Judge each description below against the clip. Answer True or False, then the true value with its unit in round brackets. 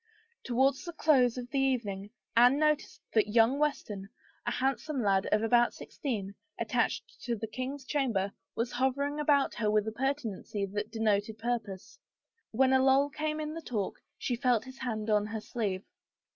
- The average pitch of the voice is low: False (245 Hz)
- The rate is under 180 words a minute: True (170 wpm)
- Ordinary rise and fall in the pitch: True (4.2 semitones)